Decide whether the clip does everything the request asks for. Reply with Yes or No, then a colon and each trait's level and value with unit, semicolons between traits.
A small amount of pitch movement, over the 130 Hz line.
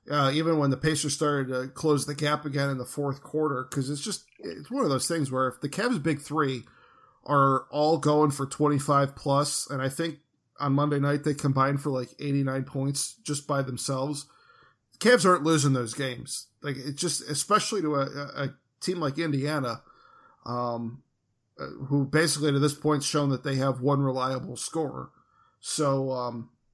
Yes: narrow, 1.9 semitones; medium, 140 Hz